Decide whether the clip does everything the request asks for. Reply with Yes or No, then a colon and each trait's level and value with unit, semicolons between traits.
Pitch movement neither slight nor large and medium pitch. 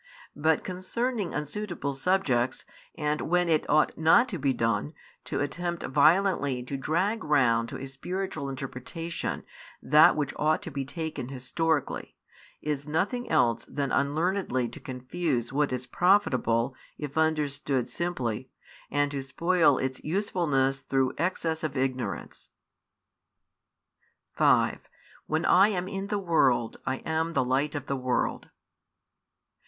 Yes: average, 4.6 semitones; medium, 150 Hz